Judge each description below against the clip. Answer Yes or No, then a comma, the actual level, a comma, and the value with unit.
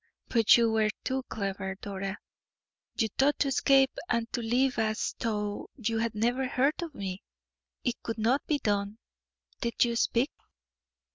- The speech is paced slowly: No, average, 155 wpm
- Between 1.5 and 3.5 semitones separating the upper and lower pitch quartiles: No, average, 3.9 semitones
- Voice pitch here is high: Yes, high, 230 Hz